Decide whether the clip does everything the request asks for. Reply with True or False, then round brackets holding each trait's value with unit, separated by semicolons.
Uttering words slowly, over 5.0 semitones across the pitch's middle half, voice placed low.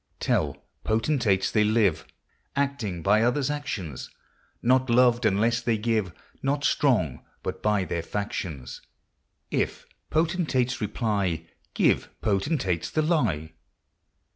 True (115 wpm; 5.4 semitones; 110 Hz)